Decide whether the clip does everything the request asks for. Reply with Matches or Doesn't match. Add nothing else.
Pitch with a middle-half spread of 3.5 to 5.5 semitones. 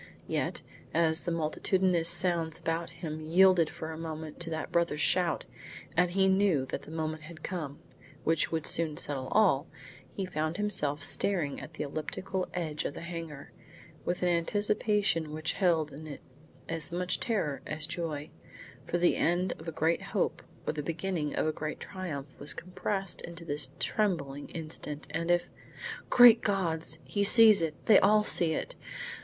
Doesn't match